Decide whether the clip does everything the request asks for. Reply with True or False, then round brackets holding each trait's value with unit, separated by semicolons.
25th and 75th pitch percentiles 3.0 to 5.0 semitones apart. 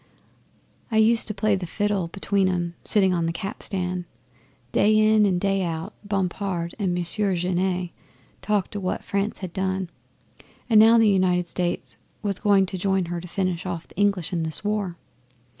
False (2.5 semitones)